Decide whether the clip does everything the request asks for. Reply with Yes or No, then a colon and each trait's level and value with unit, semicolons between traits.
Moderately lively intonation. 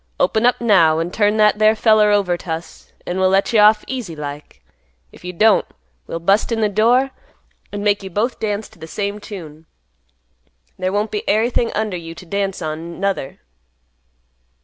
Yes: average, 3.8 semitones